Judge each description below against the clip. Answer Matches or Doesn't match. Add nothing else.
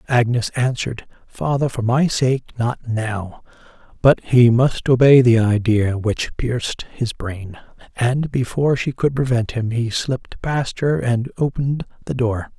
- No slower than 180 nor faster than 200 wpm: Doesn't match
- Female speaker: Doesn't match